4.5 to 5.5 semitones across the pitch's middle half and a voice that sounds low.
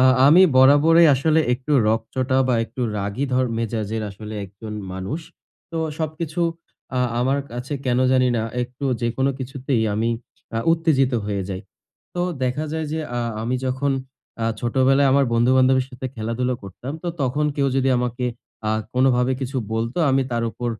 No: average, 3.0 semitones; low, 130 Hz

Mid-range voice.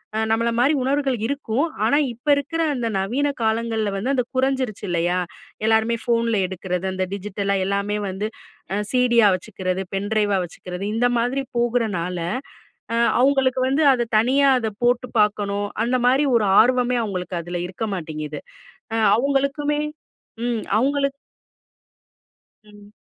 No: high, 230 Hz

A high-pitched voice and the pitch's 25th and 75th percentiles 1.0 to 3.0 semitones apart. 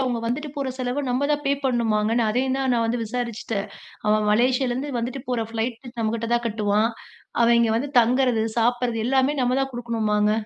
Yes: high, 240 Hz; narrow, 2.4 semitones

